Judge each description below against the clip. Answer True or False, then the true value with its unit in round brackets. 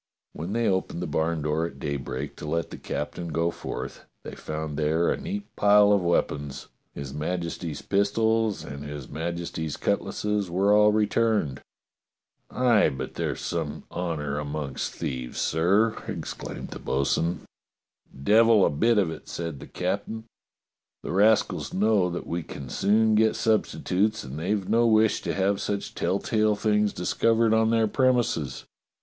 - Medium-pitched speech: False (95 Hz)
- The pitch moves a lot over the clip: True (5.8 semitones)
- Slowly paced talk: False (155 wpm)